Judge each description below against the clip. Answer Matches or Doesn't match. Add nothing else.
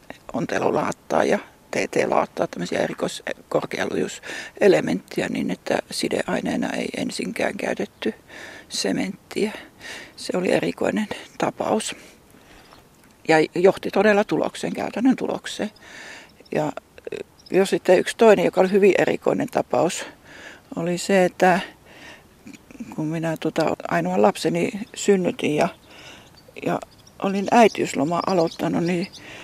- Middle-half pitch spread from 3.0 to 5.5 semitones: Matches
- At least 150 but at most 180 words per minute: Doesn't match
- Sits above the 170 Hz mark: Matches